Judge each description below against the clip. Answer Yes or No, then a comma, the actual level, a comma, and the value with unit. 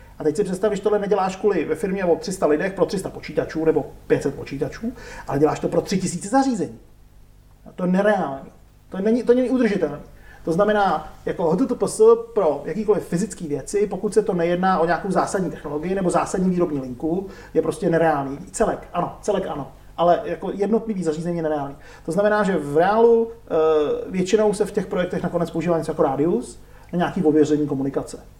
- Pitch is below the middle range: No, medium, 175 Hz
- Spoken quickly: Yes, fast, 185 wpm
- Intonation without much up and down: No, average, 5.0 semitones